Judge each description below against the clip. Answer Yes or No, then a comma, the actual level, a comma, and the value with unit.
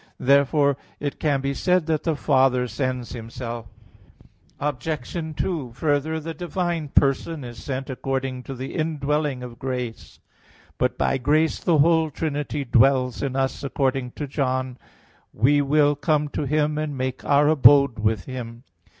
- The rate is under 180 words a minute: Yes, average, 150 wpm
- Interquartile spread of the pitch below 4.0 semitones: Yes, average, 2.9 semitones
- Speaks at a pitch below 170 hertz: Yes, medium, 140 Hz